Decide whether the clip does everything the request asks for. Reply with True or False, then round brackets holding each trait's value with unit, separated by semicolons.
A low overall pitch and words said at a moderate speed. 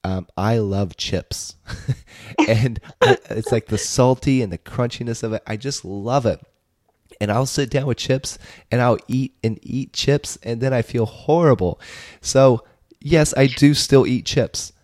True (120 Hz; 170 wpm)